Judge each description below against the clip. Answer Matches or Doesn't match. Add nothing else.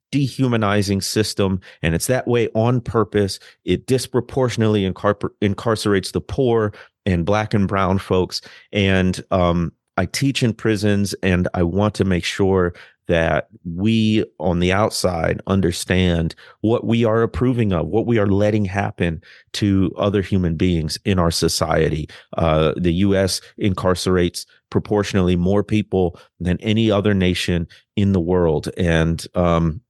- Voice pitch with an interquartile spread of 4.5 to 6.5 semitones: Doesn't match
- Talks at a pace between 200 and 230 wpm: Doesn't match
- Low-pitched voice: Matches